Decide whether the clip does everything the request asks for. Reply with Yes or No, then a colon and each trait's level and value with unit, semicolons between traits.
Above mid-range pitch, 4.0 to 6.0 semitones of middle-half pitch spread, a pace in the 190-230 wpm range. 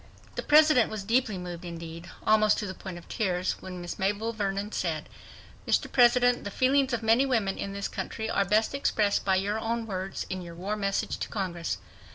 No: high, 200 Hz; average, 3.5 semitones; average, 200 wpm